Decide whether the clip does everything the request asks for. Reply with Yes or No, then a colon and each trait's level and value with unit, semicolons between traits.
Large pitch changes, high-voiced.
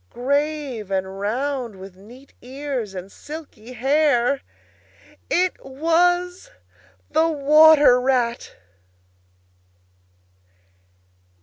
No: average, 4.6 semitones; very high, 270 Hz